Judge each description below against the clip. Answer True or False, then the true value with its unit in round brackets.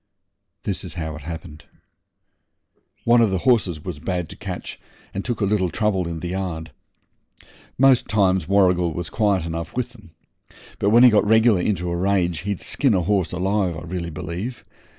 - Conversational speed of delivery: True (180 wpm)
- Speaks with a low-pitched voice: True (95 Hz)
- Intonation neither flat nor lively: True (3.8 semitones)